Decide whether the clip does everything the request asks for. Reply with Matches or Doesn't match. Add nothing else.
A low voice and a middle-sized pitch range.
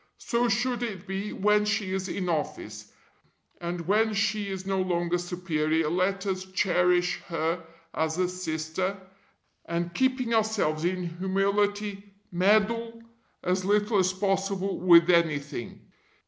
Doesn't match